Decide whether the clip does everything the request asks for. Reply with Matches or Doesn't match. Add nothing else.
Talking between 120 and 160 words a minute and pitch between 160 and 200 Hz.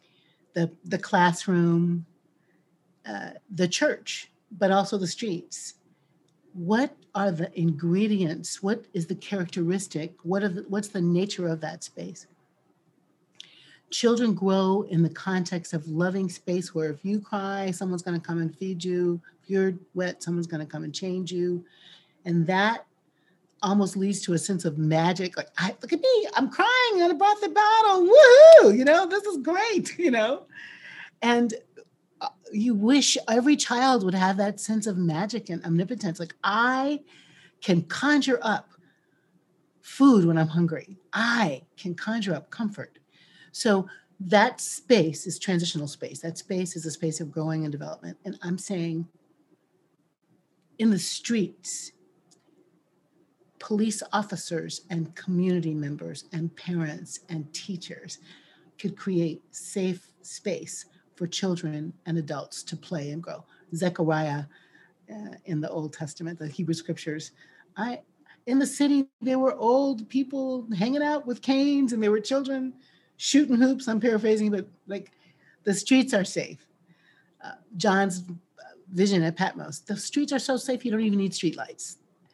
Matches